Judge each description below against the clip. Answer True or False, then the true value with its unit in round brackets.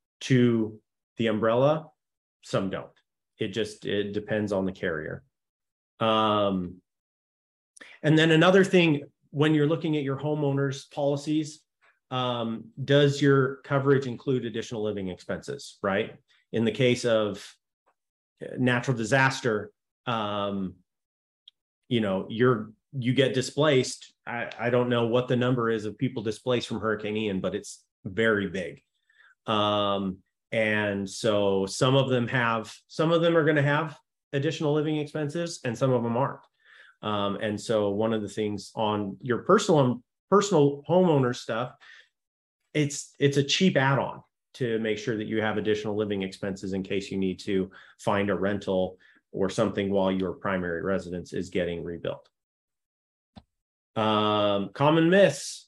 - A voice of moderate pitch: False (115 Hz)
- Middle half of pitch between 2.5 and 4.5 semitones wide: False (5.3 semitones)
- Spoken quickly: False (145 wpm)